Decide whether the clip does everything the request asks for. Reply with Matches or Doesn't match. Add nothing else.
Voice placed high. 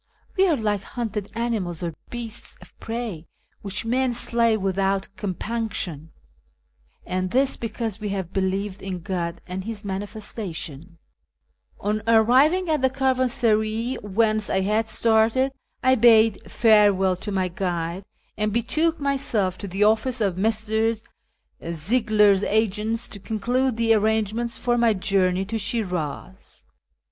Matches